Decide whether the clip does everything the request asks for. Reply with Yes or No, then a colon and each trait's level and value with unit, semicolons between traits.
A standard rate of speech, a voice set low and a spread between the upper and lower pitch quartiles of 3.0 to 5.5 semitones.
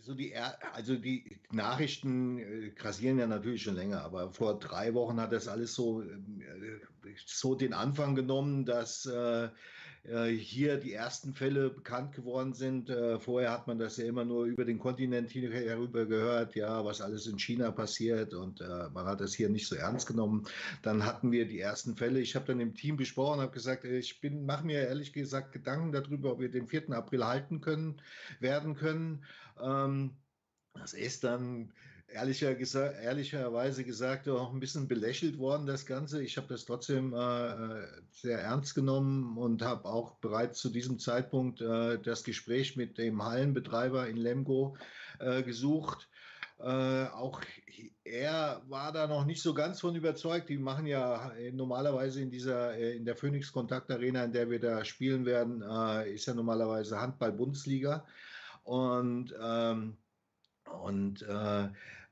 No: average, 160 wpm; low, 125 Hz; narrow, 2.6 semitones